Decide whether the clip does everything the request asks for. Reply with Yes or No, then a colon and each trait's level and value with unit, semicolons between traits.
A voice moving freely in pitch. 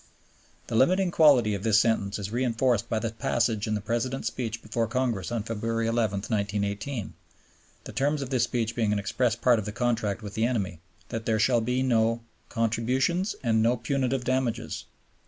No: narrow, 2.6 semitones